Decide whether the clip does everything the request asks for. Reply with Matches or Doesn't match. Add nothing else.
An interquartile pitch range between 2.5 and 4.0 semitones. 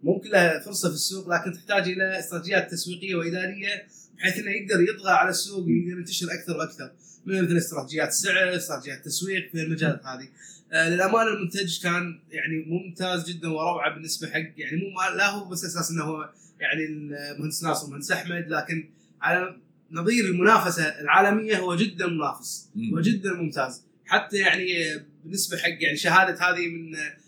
Matches